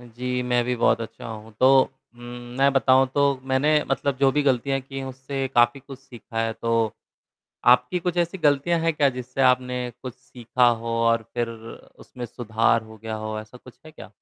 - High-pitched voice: No, low, 125 Hz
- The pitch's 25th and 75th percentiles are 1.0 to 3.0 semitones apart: Yes, average, 2.7 semitones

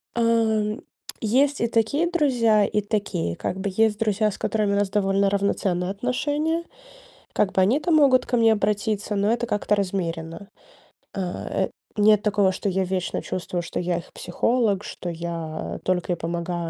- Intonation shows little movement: No, average, 3.6 semitones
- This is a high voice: Yes, high, 205 Hz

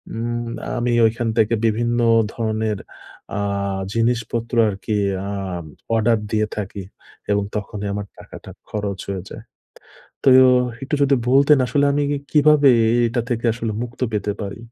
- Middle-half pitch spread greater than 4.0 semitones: No, average, 2.7 semitones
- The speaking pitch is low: Yes, low, 115 Hz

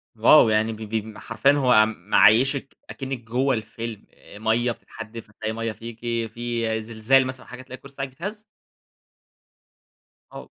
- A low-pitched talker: Yes, low, 115 Hz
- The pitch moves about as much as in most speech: Yes, average, 3.0 semitones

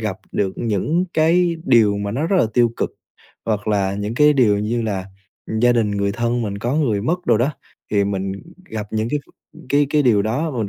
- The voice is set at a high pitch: No, low, 115 Hz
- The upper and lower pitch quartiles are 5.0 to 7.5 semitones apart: Yes, average, 5.3 semitones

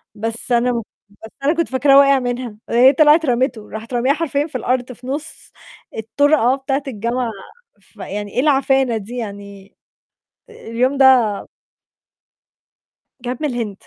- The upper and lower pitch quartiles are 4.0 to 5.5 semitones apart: No, average, 3.2 semitones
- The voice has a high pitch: Yes, very high, 250 Hz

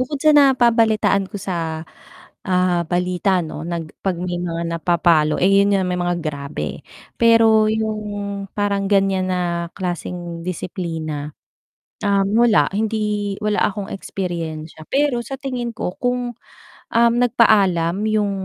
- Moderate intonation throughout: Yes, average, 4.0 semitones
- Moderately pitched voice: No, high, 195 Hz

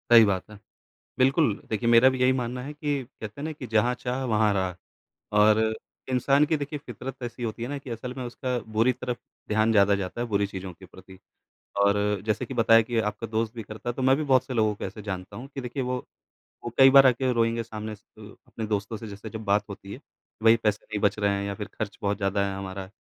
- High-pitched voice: No, low, 115 Hz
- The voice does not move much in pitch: No, average, 3.6 semitones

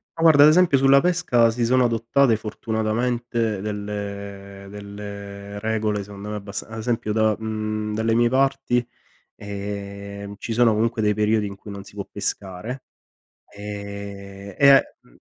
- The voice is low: Yes, low, 105 Hz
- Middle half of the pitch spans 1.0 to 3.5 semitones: Yes, narrow, 2.6 semitones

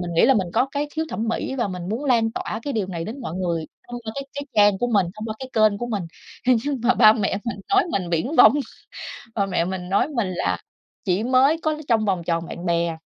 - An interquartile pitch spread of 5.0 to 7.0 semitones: Yes, wide, 5.4 semitones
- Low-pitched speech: No, high, 215 Hz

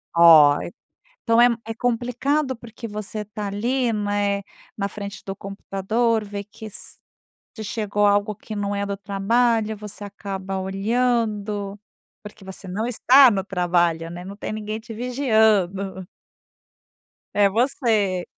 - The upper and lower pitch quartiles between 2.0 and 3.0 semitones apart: Yes, narrow, 2.5 semitones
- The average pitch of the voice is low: No, high, 205 Hz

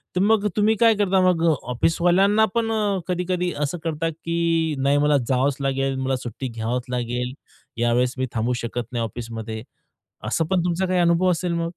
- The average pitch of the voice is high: No, medium, 160 Hz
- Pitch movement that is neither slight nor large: No, wide, 6.4 semitones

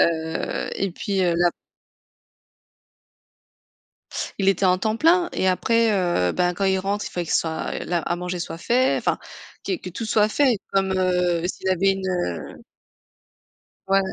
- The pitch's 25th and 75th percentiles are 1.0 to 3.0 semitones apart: Yes, narrow, 2.6 semitones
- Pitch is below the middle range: No, medium, 185 Hz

